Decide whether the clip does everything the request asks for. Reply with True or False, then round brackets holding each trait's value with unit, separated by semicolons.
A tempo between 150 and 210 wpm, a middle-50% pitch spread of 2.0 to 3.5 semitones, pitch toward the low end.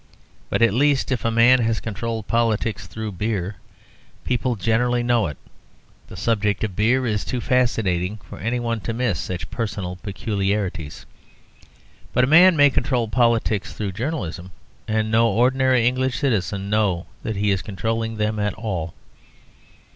True (155 wpm; 3.2 semitones; 110 Hz)